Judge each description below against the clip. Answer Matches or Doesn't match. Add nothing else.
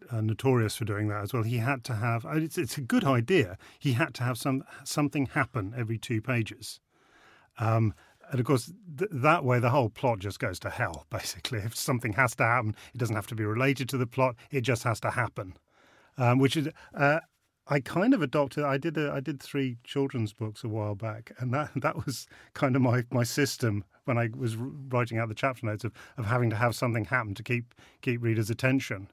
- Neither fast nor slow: Doesn't match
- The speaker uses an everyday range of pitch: Matches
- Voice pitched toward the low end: Matches